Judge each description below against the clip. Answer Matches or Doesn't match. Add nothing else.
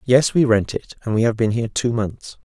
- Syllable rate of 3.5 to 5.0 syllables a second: Doesn't match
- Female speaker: Doesn't match